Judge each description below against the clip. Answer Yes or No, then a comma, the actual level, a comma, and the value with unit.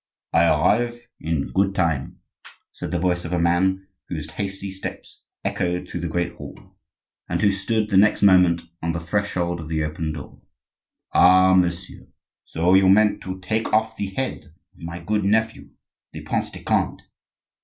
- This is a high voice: No, very low, 90 Hz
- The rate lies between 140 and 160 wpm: No, average, 170 wpm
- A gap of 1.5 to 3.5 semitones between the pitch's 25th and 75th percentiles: Yes, average, 2.8 semitones